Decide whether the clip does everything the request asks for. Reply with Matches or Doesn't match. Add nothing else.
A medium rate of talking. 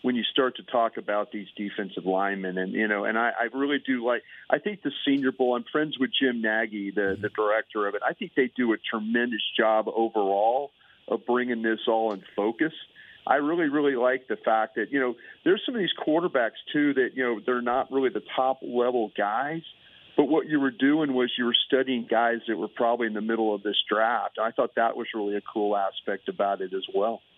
Doesn't match